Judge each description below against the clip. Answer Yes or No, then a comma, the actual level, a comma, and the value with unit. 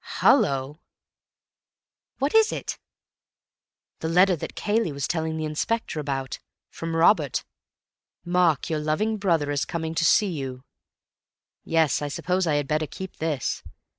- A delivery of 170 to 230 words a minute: No, slow, 135 wpm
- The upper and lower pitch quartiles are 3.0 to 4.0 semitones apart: Yes, average, 3.6 semitones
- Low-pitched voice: No, medium, 160 Hz